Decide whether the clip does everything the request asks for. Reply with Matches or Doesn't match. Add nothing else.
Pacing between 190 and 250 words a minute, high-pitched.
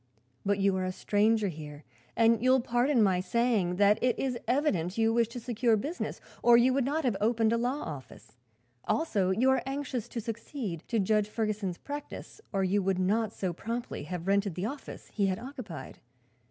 Matches